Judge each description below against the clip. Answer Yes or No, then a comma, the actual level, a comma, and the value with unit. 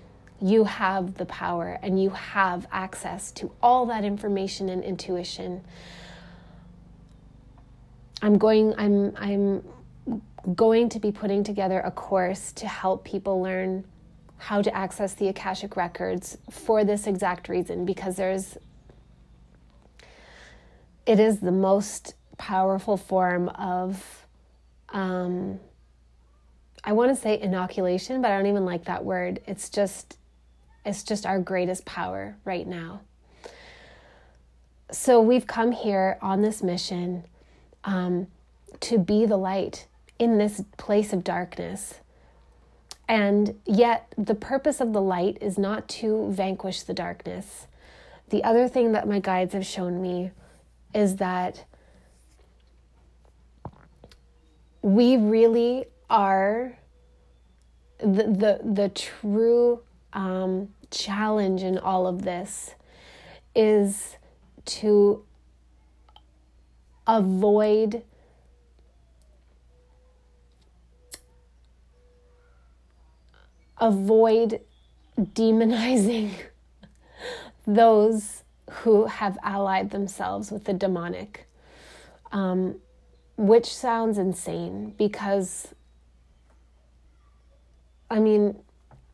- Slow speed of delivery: Yes, slow, 95 wpm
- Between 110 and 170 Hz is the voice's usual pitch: No, high, 190 Hz